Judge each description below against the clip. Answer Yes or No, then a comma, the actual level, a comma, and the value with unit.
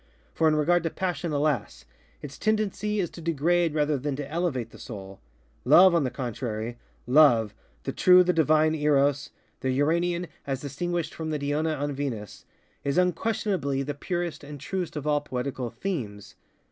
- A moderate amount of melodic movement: Yes, average, 4.2 semitones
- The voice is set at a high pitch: No, medium, 150 Hz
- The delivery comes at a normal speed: Yes, average, 150 wpm